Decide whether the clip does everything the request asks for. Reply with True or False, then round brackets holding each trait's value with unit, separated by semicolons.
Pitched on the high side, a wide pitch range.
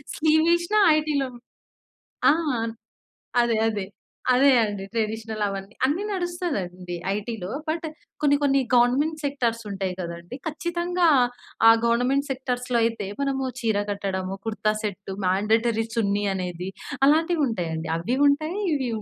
True (235 Hz; 6.4 semitones)